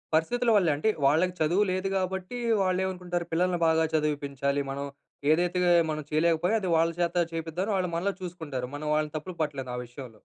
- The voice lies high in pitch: No, medium, 165 Hz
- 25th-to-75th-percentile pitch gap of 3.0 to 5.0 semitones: Yes, average, 3.3 semitones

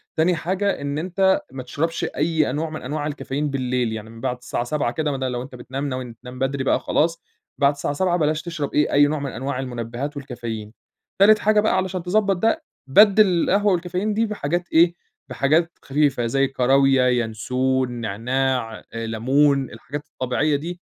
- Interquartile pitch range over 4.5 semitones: Yes, average, 4.9 semitones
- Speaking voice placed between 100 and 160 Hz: Yes, medium, 140 Hz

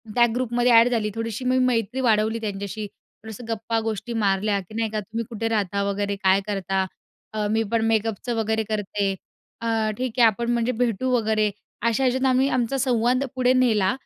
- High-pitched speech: Yes, high, 225 Hz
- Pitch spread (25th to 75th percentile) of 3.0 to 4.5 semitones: No, narrow, 2.4 semitones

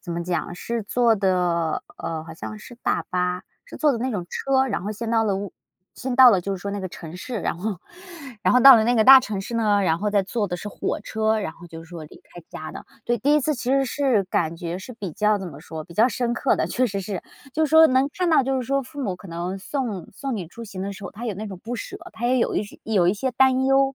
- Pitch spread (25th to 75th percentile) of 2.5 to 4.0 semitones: No, wide, 5.5 semitones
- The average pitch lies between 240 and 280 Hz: No, high, 210 Hz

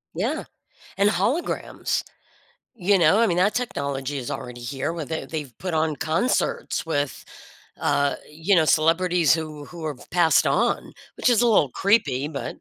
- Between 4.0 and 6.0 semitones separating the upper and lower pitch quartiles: Yes, average, 4.4 semitones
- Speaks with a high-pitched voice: No, medium, 160 Hz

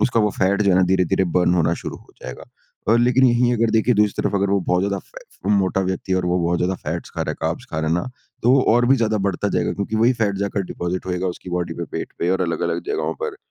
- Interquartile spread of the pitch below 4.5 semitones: Yes, average, 3.8 semitones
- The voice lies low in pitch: Yes, very low, 95 Hz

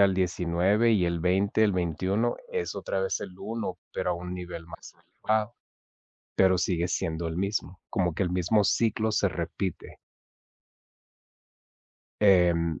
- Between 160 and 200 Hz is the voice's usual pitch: No, very low, 90 Hz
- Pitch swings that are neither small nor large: Yes, average, 3.2 semitones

